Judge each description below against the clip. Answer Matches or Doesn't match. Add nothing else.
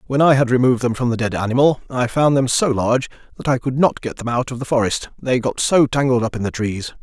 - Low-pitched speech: Matches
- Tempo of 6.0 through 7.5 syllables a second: Matches